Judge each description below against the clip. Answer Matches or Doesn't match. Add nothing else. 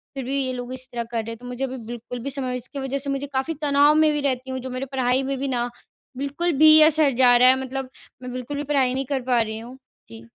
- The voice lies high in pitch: Matches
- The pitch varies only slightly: Matches